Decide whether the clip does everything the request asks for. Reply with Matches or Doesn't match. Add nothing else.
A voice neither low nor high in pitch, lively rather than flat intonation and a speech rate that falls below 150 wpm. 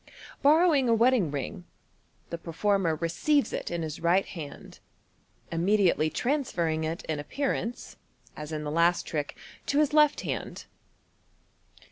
Matches